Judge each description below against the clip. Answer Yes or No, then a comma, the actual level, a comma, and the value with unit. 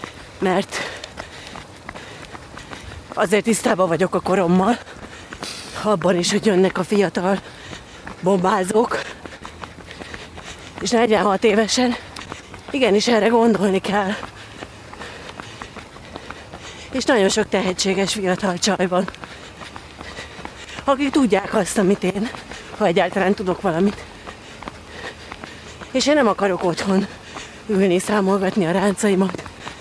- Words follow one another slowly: Yes, slow, 90 wpm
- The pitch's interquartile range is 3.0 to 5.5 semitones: No, narrow, 2.6 semitones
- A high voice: Yes, high, 195 Hz